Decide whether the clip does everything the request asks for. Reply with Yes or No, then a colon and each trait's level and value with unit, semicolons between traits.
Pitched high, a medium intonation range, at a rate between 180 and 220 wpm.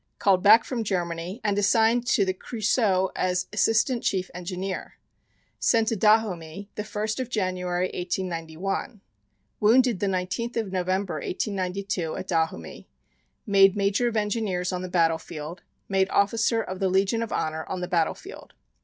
No: high, 195 Hz; average, 3.1 semitones; average, 155 wpm